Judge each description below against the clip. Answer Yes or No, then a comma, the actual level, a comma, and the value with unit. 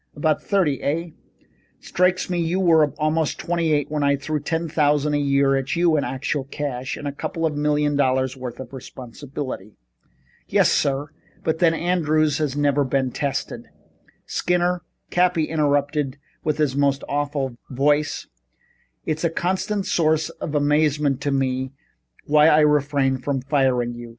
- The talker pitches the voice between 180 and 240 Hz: No, medium, 145 Hz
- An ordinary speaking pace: Yes, average, 155 wpm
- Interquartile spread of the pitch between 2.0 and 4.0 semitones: Yes, narrow, 2.4 semitones